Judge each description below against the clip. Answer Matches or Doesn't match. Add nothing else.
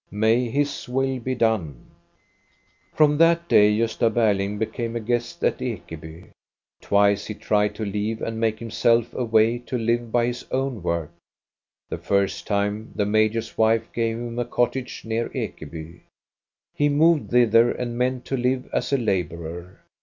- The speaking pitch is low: Matches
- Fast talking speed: Doesn't match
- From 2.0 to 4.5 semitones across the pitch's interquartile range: Matches